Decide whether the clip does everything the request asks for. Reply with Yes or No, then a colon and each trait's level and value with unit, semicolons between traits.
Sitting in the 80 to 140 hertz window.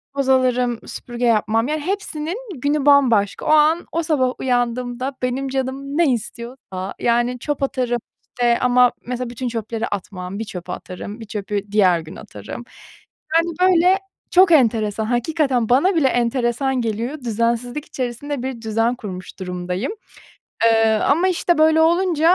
No: high, 245 Hz